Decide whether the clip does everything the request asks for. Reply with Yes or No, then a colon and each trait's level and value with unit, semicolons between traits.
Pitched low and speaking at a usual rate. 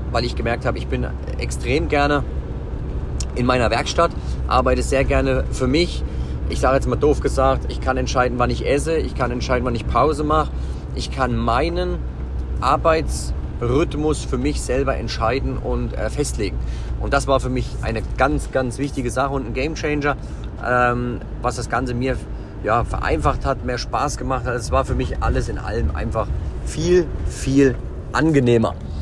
Yes: low, 115 Hz; average, 170 wpm